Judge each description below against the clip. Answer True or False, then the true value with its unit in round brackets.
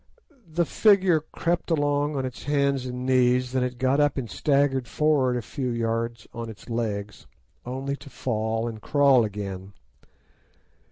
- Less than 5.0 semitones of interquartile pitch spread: True (3.6 semitones)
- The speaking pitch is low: True (130 Hz)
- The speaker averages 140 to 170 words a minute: True (155 wpm)